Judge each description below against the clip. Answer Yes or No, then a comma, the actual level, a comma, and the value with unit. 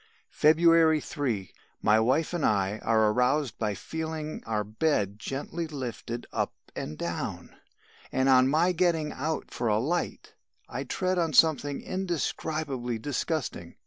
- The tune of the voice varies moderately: No, wide, 6.3 semitones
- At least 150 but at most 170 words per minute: No, slow, 135 wpm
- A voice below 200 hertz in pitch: Yes, medium, 140 Hz